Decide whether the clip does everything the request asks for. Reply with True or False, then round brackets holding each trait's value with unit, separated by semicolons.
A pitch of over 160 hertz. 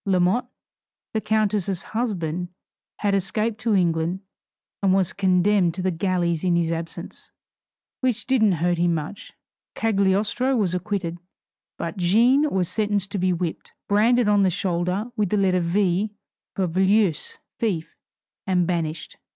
True (190 Hz)